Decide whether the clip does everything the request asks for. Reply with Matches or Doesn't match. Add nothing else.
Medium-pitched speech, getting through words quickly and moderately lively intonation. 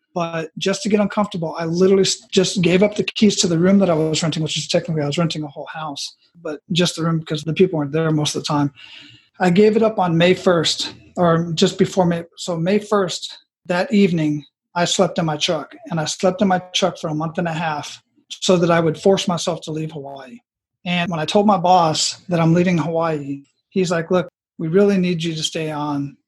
Matches